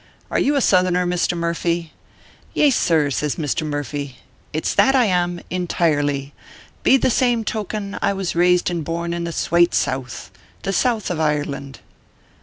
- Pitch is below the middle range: No, medium, 170 Hz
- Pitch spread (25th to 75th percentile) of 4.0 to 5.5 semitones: Yes, average, 4.3 semitones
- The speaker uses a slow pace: No, average, 185 wpm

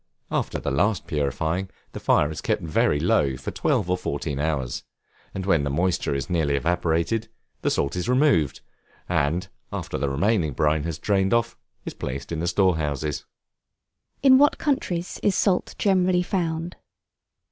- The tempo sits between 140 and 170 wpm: Yes, average, 160 wpm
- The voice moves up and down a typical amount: No, wide, 7.5 semitones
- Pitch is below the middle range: Yes, very low, 85 Hz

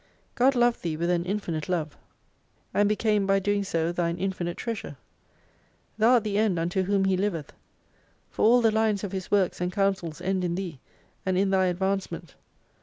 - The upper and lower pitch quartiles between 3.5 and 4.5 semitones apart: No, average, 2.9 semitones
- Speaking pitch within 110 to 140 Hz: No, high, 190 Hz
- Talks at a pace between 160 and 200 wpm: Yes, average, 185 wpm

